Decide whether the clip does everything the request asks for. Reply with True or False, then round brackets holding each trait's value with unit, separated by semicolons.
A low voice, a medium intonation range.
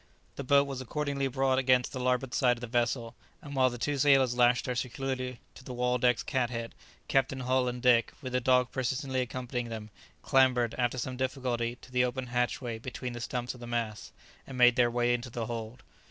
False (125 Hz; 1.4 semitones)